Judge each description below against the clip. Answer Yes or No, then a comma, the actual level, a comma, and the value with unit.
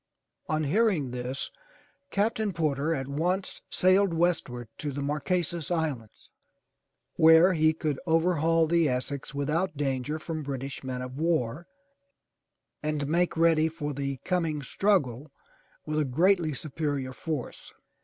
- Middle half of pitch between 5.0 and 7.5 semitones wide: No, average, 3.4 semitones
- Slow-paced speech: Yes, slow, 130 wpm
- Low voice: No, medium, 155 Hz